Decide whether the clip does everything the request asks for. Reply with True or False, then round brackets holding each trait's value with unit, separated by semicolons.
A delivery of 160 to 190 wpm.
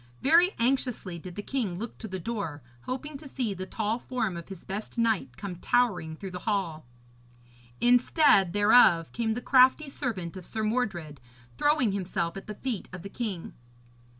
True (175 wpm)